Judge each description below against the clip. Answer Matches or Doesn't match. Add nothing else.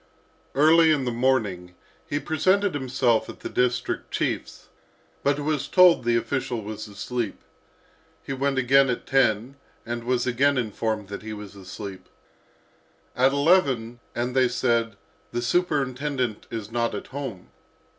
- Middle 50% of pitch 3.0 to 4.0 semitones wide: Matches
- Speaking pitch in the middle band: Doesn't match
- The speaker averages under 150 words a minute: Matches